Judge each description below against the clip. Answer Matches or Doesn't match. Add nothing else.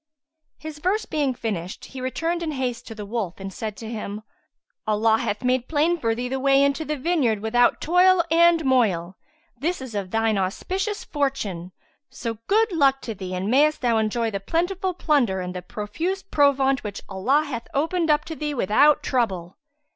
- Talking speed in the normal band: Matches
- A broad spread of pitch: Matches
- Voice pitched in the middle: Doesn't match